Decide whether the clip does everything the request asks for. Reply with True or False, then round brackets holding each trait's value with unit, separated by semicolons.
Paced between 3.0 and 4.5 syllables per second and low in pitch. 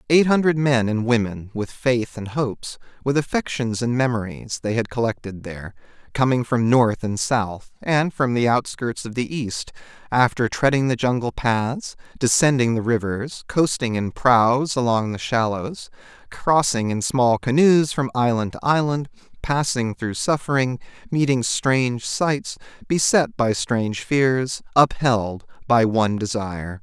True (4.3 syllables/s; 125 Hz)